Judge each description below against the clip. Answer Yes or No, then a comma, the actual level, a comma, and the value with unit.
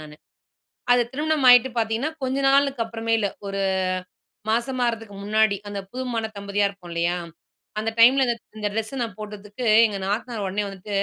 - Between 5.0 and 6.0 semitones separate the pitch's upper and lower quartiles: No, average, 3.6 semitones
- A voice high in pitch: Yes, high, 220 Hz